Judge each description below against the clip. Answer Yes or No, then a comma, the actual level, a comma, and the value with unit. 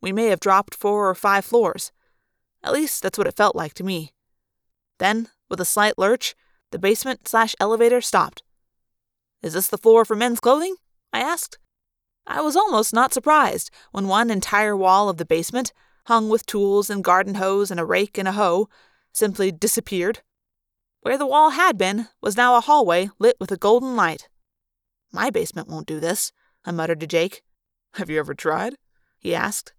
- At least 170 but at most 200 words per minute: Yes, average, 185 wpm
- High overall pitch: Yes, high, 205 Hz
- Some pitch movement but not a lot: Yes, average, 4.4 semitones